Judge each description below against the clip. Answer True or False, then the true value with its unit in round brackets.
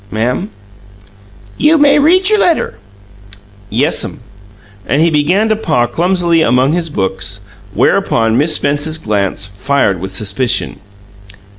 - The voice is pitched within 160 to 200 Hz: False (145 Hz)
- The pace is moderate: False (120 wpm)